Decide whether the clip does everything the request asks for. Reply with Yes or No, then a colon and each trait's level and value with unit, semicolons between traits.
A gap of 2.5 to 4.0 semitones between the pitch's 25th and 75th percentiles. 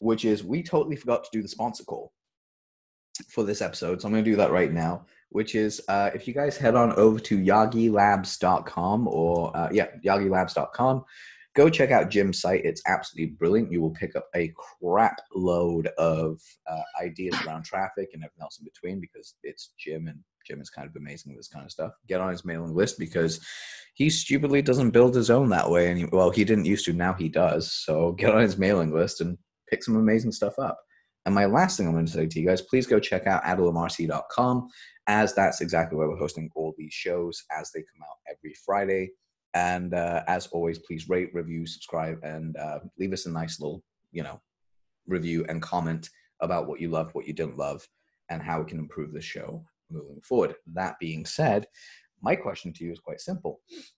No: average, 4.8 semitones